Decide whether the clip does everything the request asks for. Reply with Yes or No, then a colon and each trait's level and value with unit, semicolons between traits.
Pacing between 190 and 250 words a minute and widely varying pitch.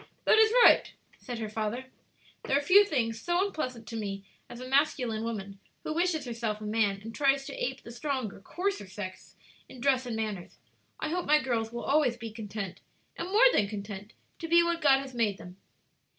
Yes: average, 200 wpm; wide, 5.9 semitones